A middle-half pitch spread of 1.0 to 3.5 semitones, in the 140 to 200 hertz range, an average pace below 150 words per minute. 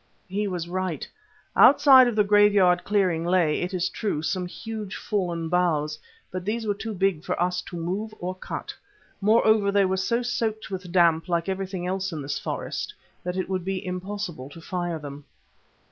No: average, 2.9 semitones; medium, 185 Hz; average, 175 wpm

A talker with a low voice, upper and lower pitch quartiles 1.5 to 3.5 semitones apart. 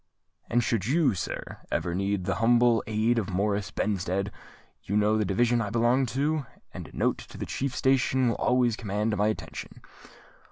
Yes: low, 110 Hz; average, 3.2 semitones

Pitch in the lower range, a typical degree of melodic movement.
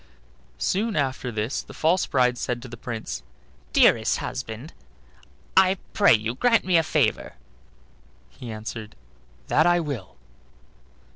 No: low, 125 Hz; wide, 7.0 semitones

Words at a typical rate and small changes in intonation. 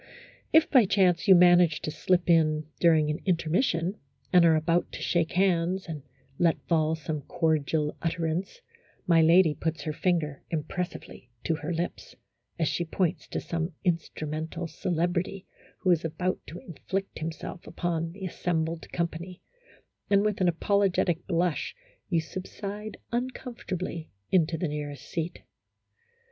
Yes: average, 145 wpm; narrow, 2.3 semitones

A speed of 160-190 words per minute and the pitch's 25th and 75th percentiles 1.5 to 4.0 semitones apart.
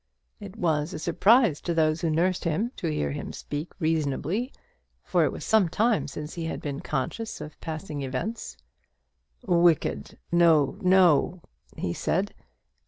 No: average, 150 wpm; average, 3.7 semitones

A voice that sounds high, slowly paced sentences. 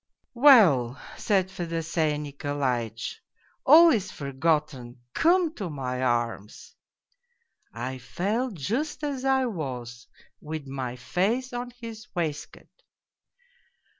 No: medium, 160 Hz; slow, 115 wpm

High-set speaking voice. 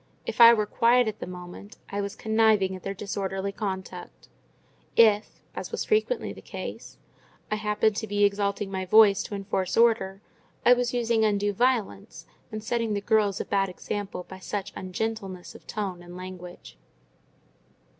Yes: high, 205 Hz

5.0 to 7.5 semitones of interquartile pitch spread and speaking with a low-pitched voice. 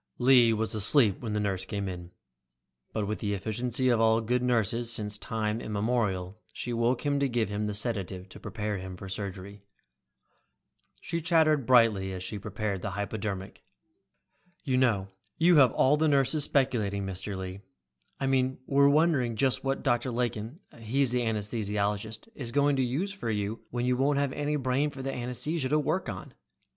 No: average, 4.5 semitones; low, 115 Hz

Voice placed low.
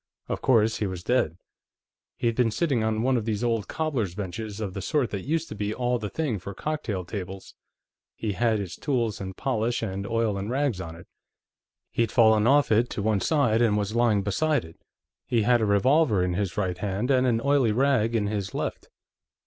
Yes: low, 110 Hz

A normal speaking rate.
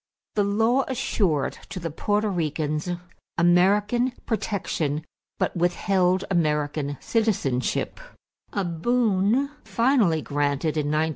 No: slow, 100 wpm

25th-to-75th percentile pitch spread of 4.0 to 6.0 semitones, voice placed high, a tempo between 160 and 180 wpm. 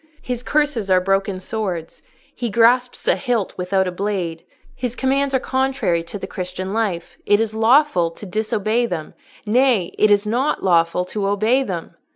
Yes: average, 5.1 semitones; high, 210 Hz; average, 165 wpm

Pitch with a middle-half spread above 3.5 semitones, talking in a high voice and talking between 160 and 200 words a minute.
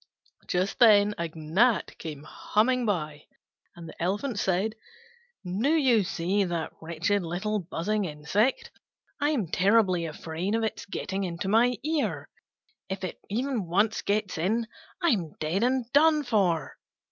No: average, 5.0 semitones; high, 200 Hz; slow, 135 wpm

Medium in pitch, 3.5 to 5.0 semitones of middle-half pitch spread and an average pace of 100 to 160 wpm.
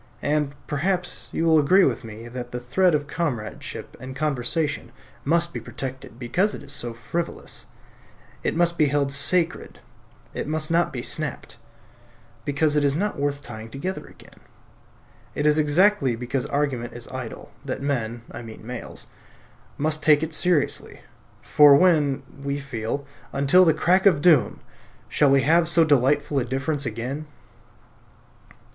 Yes: medium, 145 Hz; average, 3.8 semitones; average, 150 wpm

